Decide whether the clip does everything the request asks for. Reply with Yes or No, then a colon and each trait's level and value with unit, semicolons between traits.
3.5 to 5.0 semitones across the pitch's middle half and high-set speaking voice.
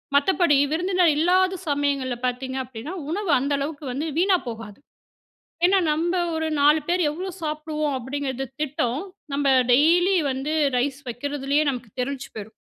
Yes: average, 4.0 semitones; very high, 290 Hz